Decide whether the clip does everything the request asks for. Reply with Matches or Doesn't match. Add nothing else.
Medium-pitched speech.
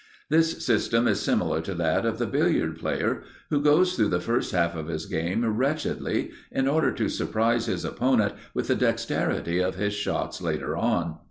Doesn't match